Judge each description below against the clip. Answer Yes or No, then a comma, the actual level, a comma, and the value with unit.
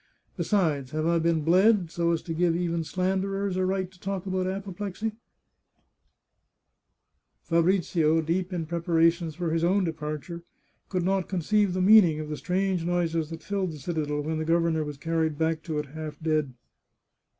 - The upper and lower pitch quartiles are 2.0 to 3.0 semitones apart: Yes, average, 2.7 semitones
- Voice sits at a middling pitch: Yes, medium, 170 Hz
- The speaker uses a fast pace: No, average, 170 wpm